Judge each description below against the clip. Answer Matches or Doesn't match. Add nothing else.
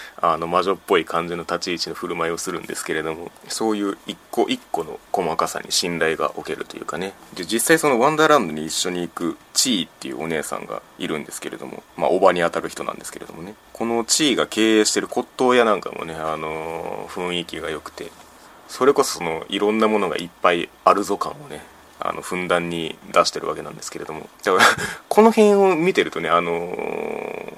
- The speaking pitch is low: Matches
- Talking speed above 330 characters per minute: Matches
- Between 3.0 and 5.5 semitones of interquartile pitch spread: Matches